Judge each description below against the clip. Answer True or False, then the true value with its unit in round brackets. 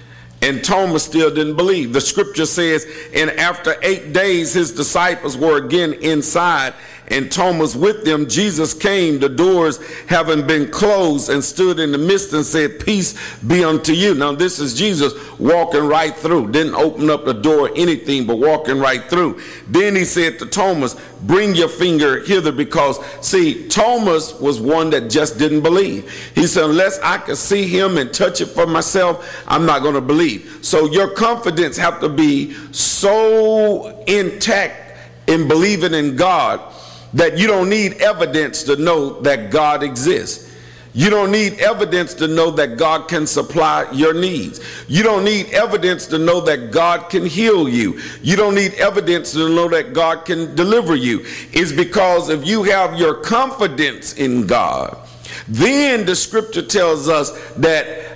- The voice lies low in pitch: False (165 Hz)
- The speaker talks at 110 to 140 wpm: False (165 wpm)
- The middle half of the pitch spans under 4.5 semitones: True (4.0 semitones)